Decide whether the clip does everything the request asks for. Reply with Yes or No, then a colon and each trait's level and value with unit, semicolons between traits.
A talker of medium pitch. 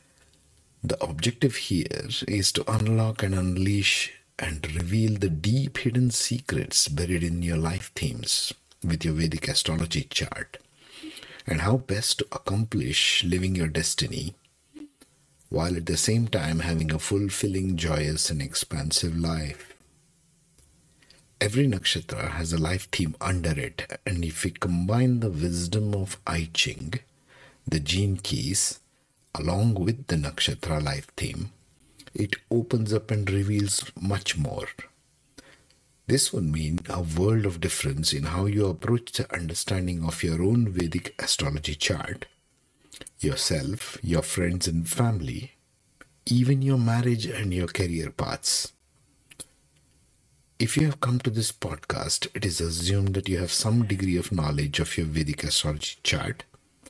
No: low, 100 Hz